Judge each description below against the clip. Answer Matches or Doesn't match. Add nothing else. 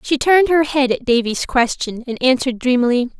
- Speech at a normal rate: Matches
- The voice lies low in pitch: Doesn't match